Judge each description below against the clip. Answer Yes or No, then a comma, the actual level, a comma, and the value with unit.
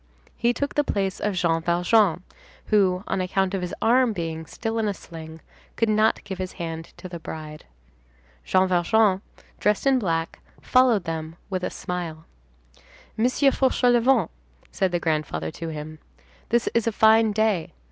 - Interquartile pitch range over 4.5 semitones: Yes, average, 5.2 semitones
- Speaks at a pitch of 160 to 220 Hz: Yes, high, 190 Hz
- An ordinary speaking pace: Yes, average, 160 wpm